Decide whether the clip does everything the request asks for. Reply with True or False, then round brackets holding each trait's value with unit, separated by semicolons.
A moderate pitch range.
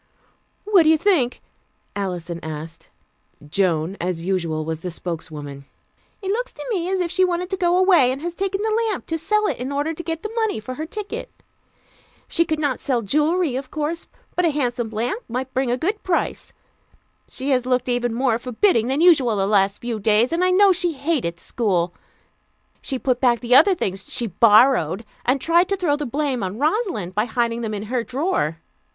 False (8.5 semitones)